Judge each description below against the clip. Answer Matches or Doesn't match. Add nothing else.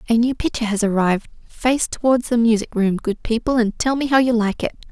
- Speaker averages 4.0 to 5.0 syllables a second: Doesn't match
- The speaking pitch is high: Matches